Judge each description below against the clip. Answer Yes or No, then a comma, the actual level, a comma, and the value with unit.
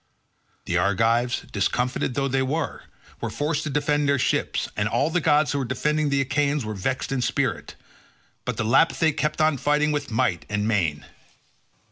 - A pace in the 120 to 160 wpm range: No, average, 175 wpm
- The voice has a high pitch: No, low, 135 Hz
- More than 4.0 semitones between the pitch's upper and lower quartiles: Yes, average, 4.4 semitones